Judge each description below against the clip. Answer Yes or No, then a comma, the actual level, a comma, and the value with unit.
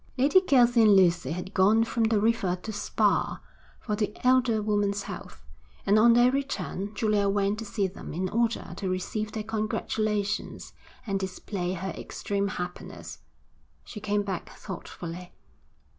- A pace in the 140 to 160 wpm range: Yes, average, 150 wpm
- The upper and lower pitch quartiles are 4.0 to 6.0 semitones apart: No, average, 2.7 semitones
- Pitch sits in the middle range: No, high, 205 Hz